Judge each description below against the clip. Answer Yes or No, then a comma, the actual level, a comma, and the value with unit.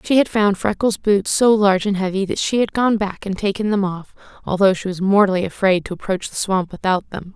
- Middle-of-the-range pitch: No, high, 195 Hz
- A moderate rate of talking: No, fast, 235 wpm